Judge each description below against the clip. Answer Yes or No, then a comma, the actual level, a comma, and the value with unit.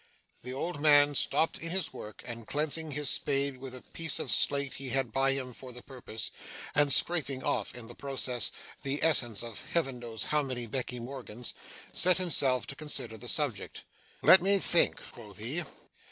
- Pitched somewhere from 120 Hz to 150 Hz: Yes, low, 135 Hz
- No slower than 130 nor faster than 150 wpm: No, average, 180 wpm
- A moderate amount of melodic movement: Yes, average, 3.4 semitones